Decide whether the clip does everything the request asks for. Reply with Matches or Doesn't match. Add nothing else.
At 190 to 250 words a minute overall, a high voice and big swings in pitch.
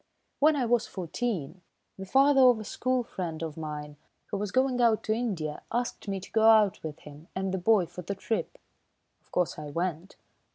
Matches